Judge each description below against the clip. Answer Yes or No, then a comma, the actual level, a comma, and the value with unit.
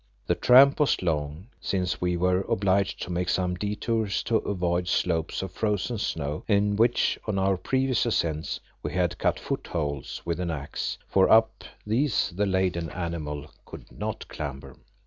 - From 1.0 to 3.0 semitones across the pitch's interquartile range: No, average, 3.7 semitones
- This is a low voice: Yes, very low, 90 Hz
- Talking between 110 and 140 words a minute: No, average, 160 wpm